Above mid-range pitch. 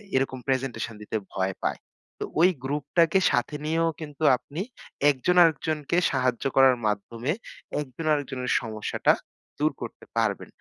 No: low, 135 Hz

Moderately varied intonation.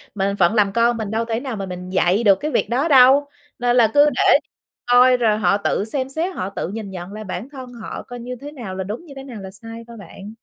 Yes: average, 4.2 semitones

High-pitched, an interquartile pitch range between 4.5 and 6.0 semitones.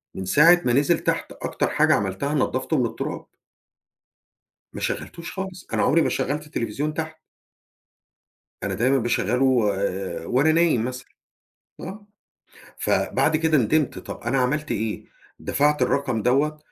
No: low, 135 Hz; average, 4.9 semitones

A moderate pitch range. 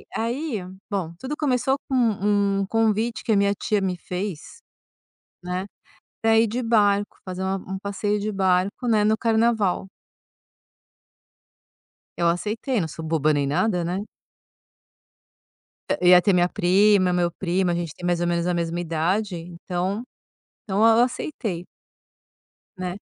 Yes: average, 3.7 semitones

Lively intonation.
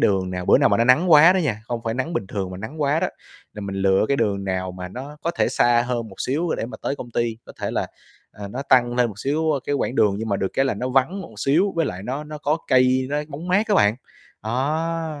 Yes: wide, 6.4 semitones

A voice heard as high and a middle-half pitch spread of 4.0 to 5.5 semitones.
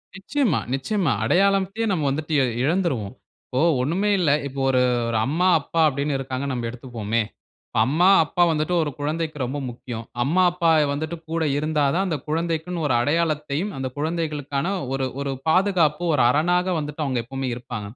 No: medium, 150 Hz; average, 4.3 semitones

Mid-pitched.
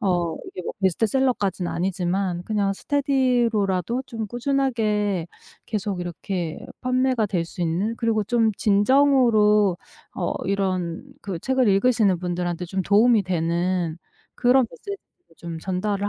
No: high, 200 Hz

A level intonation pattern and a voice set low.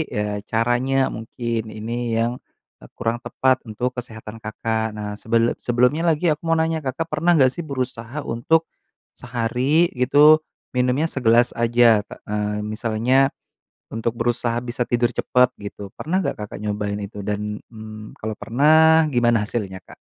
No: average, 3.0 semitones; low, 120 Hz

